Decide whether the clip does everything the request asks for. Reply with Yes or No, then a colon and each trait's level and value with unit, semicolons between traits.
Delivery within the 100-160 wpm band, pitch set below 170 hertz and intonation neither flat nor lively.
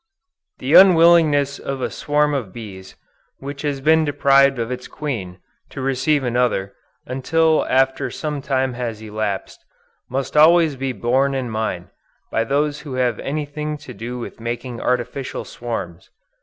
Yes: average, 145 wpm; low, 135 Hz; average, 3.6 semitones